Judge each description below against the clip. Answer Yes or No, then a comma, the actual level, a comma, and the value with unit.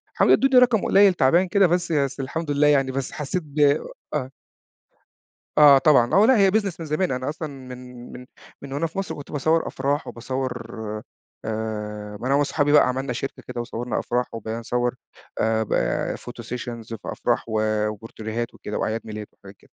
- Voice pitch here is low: Yes, low, 130 Hz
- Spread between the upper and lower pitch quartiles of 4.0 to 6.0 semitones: Yes, average, 4.6 semitones